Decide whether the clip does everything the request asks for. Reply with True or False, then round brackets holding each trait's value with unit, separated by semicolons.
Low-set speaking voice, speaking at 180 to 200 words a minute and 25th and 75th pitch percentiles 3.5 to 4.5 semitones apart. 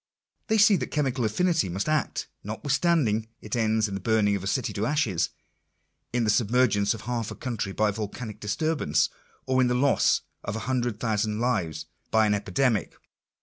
True (110 Hz; 190 wpm; 3.8 semitones)